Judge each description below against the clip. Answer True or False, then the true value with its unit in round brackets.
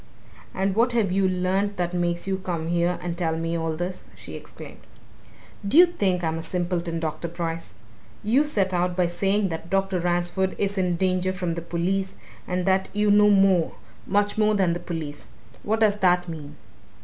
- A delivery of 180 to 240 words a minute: True (185 wpm)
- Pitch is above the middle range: False (180 Hz)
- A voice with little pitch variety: True (2.3 semitones)